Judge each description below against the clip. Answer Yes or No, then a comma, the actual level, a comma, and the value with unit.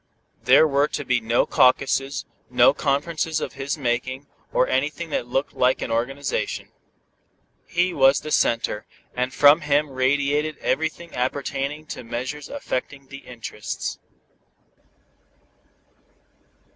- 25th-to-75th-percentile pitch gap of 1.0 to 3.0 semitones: Yes, narrow, 2.6 semitones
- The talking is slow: Yes, slow, 120 wpm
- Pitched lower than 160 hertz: Yes, medium, 140 Hz